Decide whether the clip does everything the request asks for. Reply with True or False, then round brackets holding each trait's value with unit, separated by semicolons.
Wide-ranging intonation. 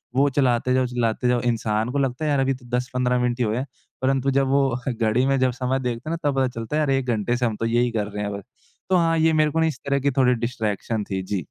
False (2.8 semitones)